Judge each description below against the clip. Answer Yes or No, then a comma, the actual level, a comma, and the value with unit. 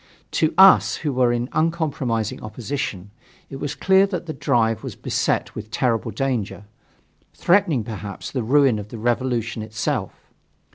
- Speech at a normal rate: Yes, average, 145 wpm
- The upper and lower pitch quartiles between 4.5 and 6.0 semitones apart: Yes, average, 4.8 semitones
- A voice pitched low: Yes, low, 120 Hz